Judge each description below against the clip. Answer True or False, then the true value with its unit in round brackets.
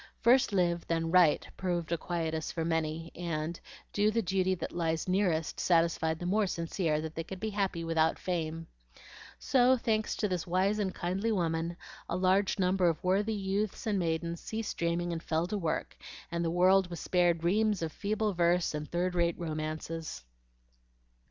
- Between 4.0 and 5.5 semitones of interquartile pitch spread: False (2.9 semitones)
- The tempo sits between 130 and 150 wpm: False (175 wpm)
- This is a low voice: False (175 Hz)